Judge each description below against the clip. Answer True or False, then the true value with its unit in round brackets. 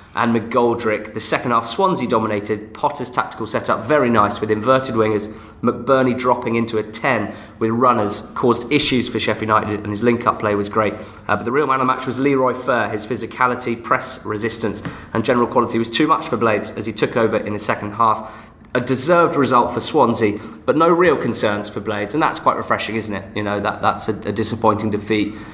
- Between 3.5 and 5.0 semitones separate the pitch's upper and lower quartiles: False (2.7 semitones)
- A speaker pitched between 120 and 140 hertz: False (110 Hz)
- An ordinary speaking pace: False (210 wpm)